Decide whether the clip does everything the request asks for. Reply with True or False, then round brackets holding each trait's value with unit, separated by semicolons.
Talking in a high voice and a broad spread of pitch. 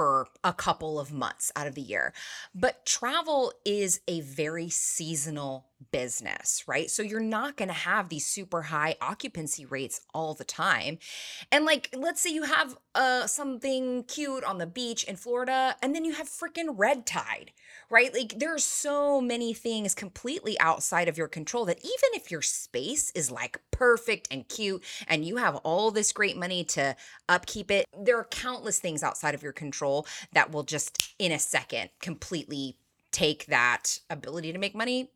True (200 Hz; 8.2 semitones)